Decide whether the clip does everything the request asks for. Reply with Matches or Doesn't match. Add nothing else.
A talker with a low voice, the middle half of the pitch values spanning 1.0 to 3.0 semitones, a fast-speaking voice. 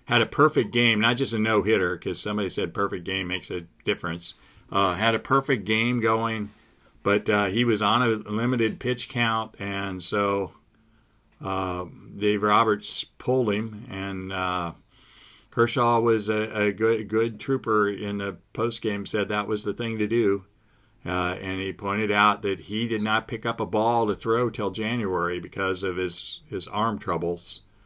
Doesn't match